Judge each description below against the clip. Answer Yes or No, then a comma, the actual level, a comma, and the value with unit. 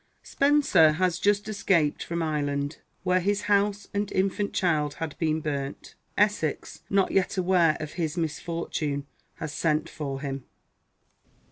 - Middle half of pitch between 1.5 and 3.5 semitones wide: No, average, 4.6 semitones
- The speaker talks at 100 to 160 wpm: Yes, slow, 135 wpm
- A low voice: No, medium, 165 Hz